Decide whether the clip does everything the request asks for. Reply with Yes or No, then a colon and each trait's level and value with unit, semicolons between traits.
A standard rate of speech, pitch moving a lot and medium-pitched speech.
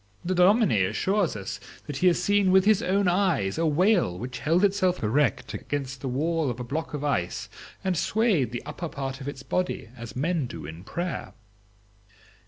Yes: average, 190 wpm; wide, 6.3 semitones; medium, 155 Hz